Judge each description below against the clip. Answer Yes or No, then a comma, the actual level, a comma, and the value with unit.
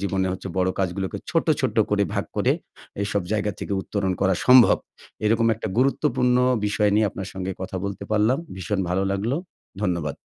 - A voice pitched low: Yes, low, 100 Hz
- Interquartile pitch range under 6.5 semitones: Yes, narrow, 2.6 semitones